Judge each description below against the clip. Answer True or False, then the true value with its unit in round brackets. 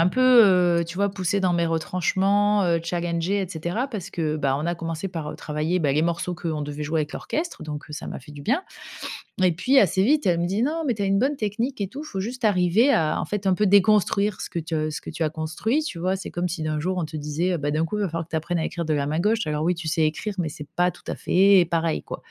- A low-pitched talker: False (175 Hz)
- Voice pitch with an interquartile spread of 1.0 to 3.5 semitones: False (4.2 semitones)